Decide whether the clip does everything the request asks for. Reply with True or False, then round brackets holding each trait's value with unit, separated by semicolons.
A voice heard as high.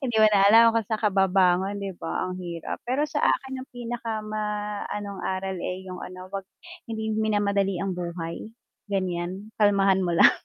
True (200 Hz)